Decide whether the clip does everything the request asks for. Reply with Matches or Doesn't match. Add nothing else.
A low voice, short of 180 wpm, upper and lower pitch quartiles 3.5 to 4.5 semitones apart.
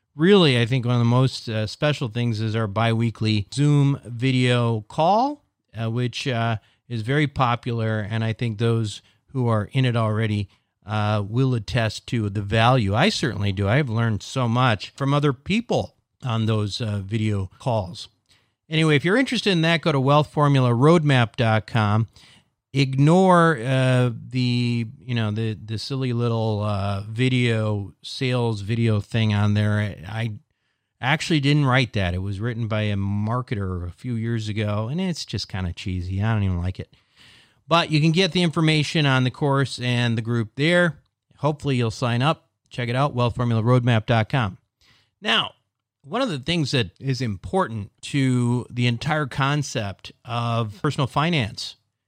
Matches